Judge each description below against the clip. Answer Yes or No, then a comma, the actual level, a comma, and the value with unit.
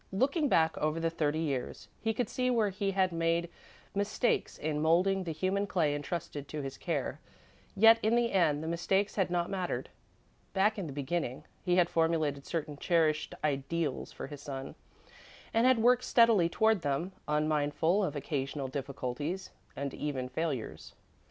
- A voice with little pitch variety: No, average, 5.0 semitones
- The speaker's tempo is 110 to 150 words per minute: No, average, 165 wpm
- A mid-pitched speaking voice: Yes, medium, 165 Hz